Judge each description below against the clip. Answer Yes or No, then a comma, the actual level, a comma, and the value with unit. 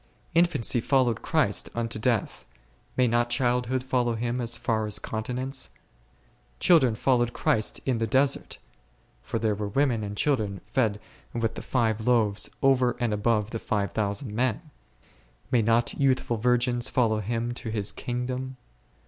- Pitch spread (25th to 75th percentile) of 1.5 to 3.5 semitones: Yes, narrow, 2.6 semitones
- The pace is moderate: Yes, average, 150 wpm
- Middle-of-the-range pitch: No, low, 120 Hz